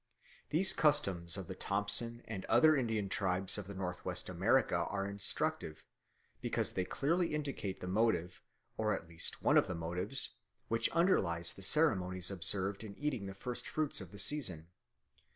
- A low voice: Yes, low, 100 Hz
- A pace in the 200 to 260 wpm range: No, average, 160 wpm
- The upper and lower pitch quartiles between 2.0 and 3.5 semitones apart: No, average, 5.1 semitones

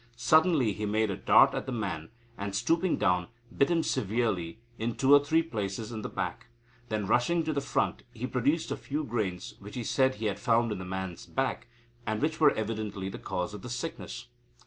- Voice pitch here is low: Yes, low, 115 Hz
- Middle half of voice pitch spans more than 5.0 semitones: Yes, wide, 5.5 semitones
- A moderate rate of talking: No, fast, 210 wpm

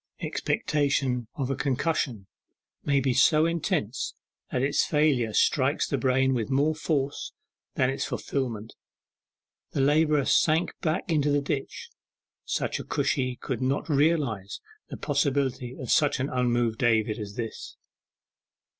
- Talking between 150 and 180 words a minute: No, slow, 135 wpm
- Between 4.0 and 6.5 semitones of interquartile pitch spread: No, average, 3.0 semitones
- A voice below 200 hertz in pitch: Yes, low, 135 Hz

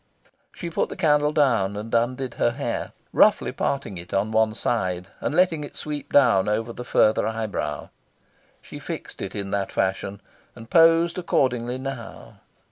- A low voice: Yes, low, 120 Hz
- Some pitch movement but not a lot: No, wide, 5.7 semitones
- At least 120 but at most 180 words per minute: Yes, average, 160 wpm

